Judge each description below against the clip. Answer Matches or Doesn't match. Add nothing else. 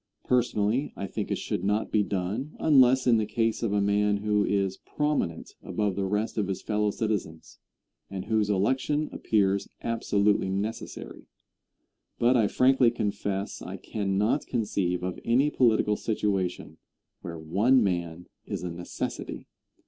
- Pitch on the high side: Doesn't match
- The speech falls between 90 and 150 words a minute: Matches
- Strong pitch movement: Doesn't match